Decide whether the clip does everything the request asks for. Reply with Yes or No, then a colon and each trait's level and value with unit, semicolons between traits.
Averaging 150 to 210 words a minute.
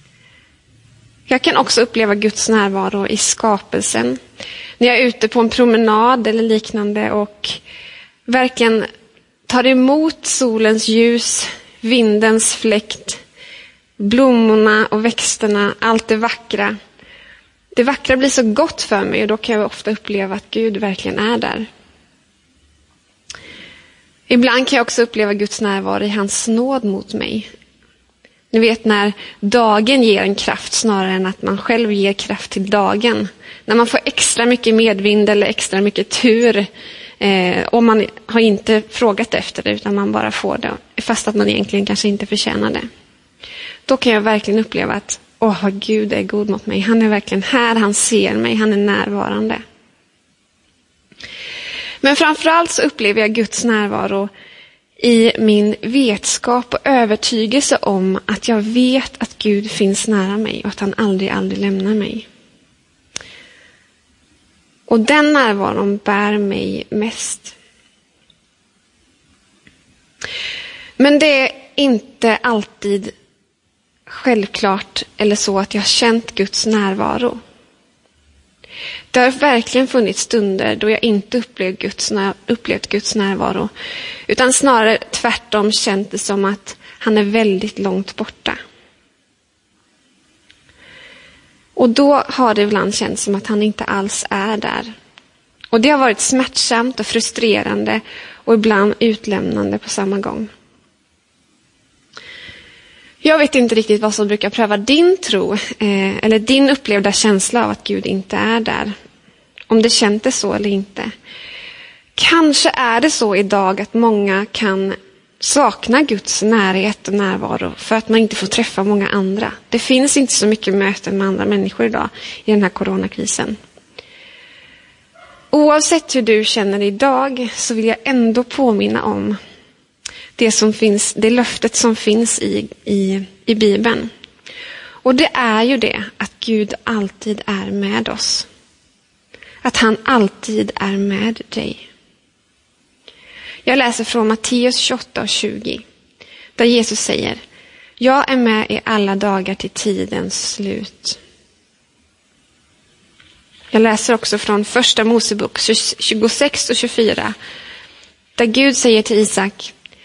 No: average, 135 wpm